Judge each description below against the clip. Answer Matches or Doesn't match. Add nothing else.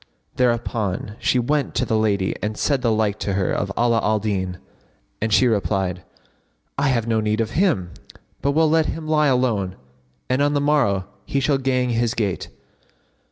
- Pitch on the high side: Doesn't match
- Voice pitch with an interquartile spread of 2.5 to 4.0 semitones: Doesn't match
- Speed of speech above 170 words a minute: Matches